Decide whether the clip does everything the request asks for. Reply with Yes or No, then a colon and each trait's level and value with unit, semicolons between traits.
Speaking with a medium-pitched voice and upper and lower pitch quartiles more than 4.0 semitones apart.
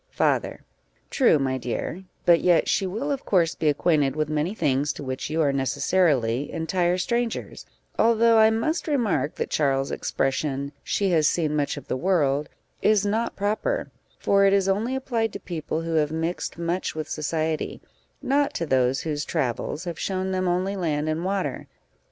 Yes: medium, 165 Hz; average, 5.2 semitones